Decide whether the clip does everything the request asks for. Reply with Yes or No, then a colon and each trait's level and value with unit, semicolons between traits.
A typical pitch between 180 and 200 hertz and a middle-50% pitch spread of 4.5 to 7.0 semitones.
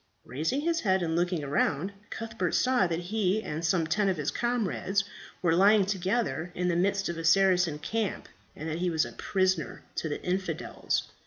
No: medium, 185 Hz; average, 3.4 semitones